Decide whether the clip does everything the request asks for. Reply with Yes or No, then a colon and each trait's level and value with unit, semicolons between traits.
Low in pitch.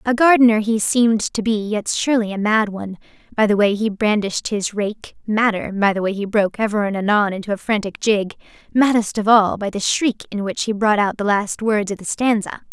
No: high, 210 Hz